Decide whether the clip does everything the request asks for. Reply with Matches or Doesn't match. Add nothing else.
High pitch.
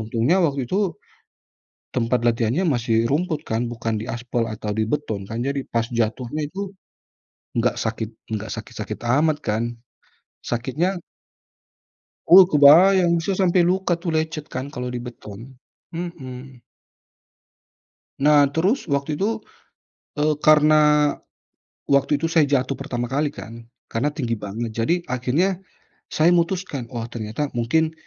Doesn't match